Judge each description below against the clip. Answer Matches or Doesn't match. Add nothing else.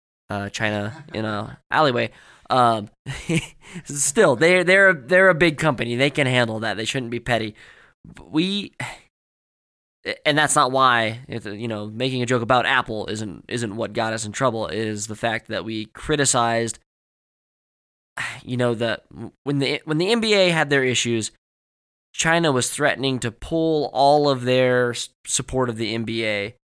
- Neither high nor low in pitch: Doesn't match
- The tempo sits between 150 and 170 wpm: Matches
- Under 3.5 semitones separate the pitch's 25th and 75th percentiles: Doesn't match